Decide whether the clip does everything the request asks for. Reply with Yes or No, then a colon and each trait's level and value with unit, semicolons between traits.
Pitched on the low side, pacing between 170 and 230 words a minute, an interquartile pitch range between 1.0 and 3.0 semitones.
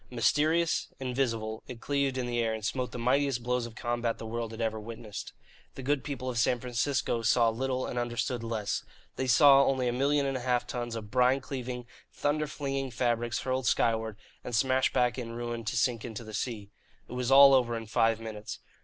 Yes: low, 120 Hz; average, 200 wpm; narrow, 2.4 semitones